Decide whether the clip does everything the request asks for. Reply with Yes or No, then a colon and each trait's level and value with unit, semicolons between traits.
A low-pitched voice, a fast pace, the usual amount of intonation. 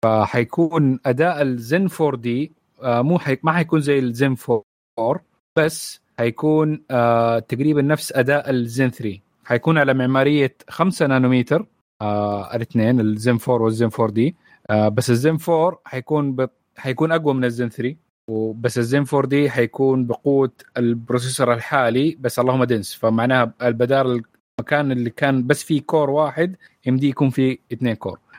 Yes: low, 130 Hz; fast, 145 wpm; average, 3.6 semitones